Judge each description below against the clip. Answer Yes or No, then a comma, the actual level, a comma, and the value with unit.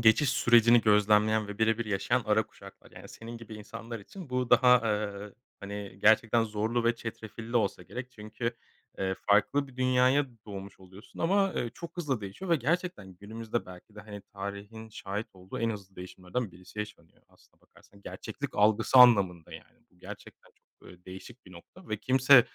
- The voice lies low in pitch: Yes, low, 110 Hz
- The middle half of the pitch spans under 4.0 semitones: Yes, average, 3.3 semitones